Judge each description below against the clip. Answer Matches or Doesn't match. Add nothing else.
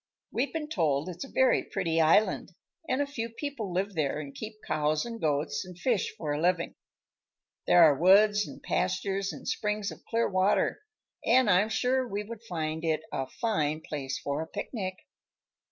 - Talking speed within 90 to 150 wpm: Doesn't match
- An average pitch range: Doesn't match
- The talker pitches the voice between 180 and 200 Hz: Matches